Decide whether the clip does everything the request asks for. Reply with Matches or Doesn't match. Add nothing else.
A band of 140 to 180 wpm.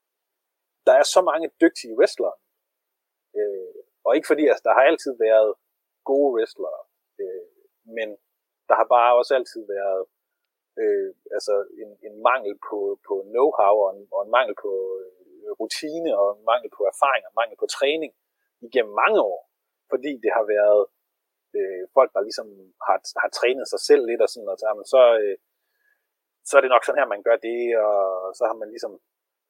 Matches